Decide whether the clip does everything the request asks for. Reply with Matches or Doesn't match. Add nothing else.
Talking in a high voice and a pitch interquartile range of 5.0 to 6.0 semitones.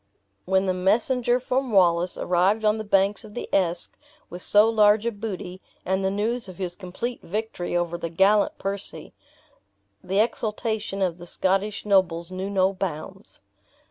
Doesn't match